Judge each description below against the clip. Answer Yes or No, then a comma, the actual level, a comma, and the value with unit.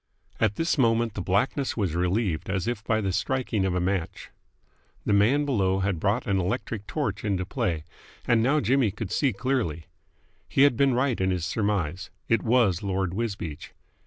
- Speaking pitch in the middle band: No, low, 105 Hz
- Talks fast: No, average, 180 wpm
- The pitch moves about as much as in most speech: Yes, average, 4.3 semitones